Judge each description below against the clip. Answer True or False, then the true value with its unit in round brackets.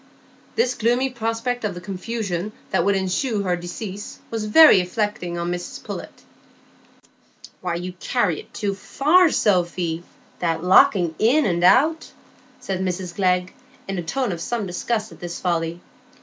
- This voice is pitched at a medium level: False (195 Hz)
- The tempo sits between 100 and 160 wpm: True (150 wpm)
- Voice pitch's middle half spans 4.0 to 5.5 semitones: True (4.4 semitones)